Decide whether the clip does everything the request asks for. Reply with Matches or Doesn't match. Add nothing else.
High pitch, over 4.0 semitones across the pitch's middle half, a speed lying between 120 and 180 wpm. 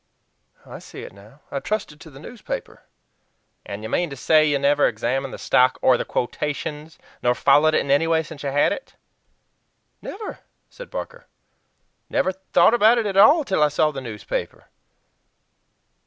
Doesn't match